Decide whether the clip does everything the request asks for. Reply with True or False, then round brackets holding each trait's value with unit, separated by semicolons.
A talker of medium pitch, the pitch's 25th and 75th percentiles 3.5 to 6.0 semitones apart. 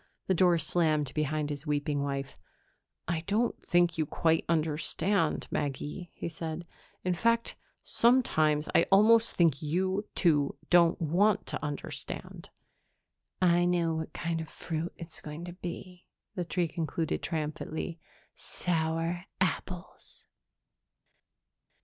False (165 Hz; 2.6 semitones)